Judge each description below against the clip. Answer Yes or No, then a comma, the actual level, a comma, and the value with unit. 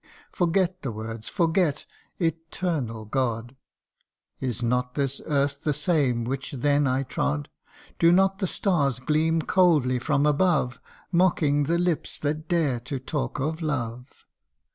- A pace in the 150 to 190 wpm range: No, slow, 135 wpm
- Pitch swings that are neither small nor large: Yes, average, 4.7 semitones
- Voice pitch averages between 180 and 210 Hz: No, medium, 145 Hz